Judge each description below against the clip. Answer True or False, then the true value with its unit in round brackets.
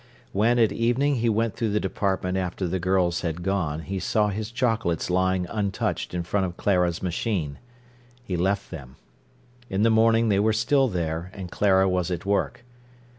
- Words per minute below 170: False (175 wpm)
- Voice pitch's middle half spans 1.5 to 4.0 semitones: True (3.7 semitones)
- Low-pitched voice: True (95 Hz)